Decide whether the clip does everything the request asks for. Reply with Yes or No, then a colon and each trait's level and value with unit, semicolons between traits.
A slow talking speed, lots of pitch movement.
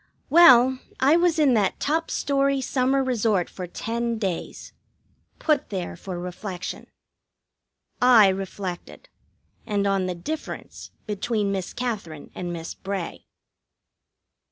Yes: slow, 115 wpm; wide, 6.0 semitones